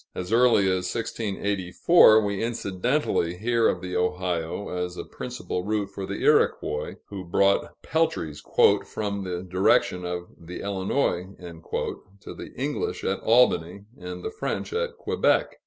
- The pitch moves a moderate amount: Yes, average, 4.1 semitones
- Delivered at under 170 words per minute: Yes, average, 140 wpm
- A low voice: Yes, very low, 95 Hz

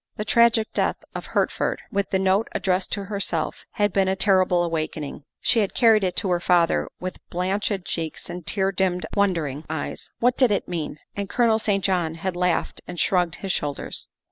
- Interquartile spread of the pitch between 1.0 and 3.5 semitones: Yes, narrow, 2.6 semitones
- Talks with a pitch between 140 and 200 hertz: Yes, high, 190 Hz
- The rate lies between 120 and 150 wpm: No, average, 195 wpm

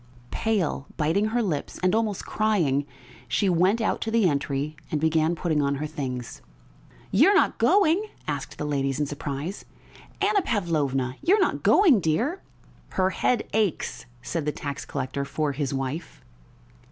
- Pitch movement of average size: No, wide, 7.3 semitones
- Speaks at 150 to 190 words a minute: Yes, average, 160 wpm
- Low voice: No, medium, 160 Hz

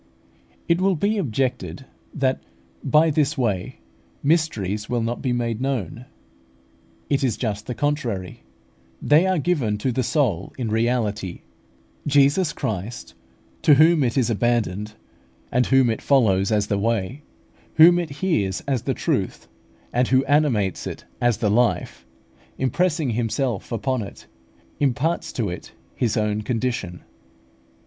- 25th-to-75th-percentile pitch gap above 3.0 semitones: Yes, average, 5.1 semitones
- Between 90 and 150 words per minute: Yes, average, 140 wpm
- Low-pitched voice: Yes, low, 125 Hz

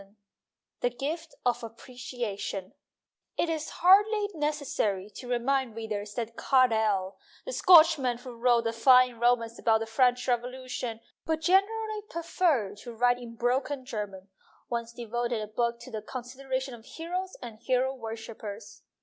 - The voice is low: No, high, 245 Hz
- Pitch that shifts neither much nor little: Yes, average, 3.2 semitones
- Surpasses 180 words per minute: No, average, 145 wpm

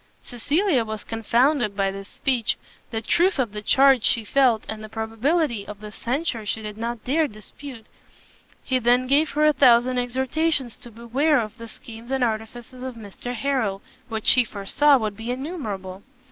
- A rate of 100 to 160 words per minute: No, average, 175 wpm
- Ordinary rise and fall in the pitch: Yes, average, 3.7 semitones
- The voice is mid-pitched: No, high, 240 Hz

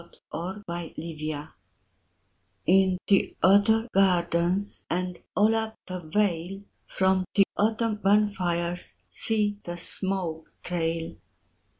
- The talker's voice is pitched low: No, medium, 185 Hz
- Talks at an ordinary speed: No, slow, 100 wpm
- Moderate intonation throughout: Yes, average, 3.1 semitones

